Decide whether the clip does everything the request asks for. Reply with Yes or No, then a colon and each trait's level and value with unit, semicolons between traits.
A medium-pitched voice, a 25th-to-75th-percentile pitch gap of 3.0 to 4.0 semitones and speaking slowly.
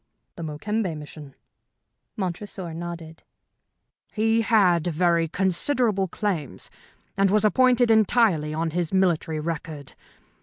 No: medium, 180 Hz; average, 4.7 semitones; slow, 105 wpm